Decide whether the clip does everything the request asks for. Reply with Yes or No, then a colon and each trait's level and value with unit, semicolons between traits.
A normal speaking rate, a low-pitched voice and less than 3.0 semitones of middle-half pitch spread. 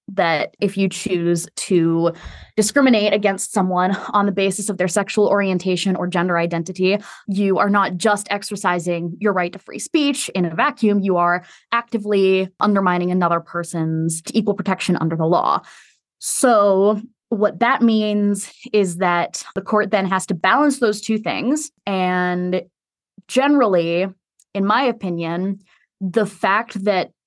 No: average, 145 wpm; high, 195 Hz; narrow, 2.6 semitones